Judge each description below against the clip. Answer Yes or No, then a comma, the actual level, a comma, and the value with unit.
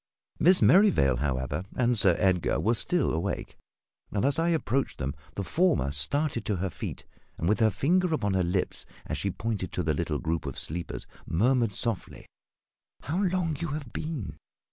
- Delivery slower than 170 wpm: No, average, 175 wpm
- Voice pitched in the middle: No, low, 110 Hz